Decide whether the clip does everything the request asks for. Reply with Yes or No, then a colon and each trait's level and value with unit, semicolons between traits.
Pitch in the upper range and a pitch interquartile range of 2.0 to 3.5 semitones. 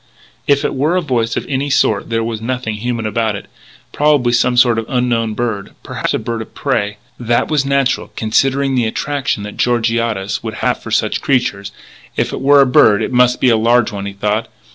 No: low, 120 Hz; average, 3.1 semitones